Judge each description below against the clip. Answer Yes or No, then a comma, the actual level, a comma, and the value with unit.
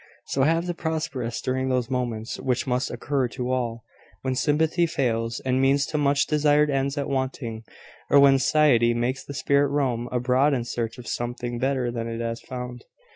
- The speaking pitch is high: No, low, 130 Hz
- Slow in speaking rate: No, average, 180 wpm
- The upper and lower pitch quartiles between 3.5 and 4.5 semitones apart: No, average, 2.7 semitones